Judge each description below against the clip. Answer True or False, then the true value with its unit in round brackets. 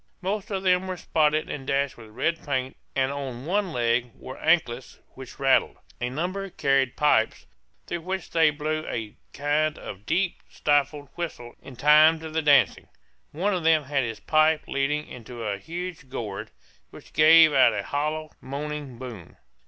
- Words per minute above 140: True (170 wpm)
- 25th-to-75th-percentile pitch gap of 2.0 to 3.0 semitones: False (3.7 semitones)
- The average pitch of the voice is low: False (150 Hz)